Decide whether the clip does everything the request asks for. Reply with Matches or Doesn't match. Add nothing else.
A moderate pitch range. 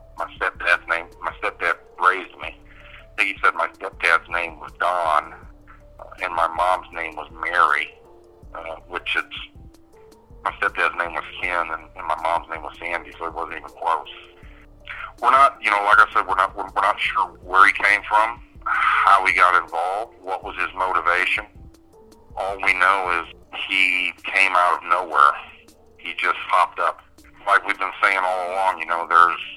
Doesn't match